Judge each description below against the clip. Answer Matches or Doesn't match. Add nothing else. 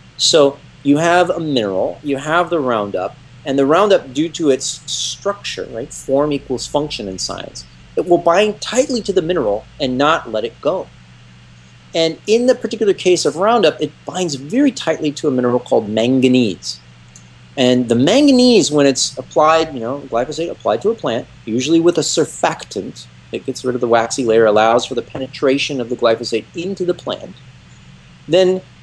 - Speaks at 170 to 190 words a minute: Matches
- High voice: Doesn't match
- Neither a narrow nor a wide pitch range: Doesn't match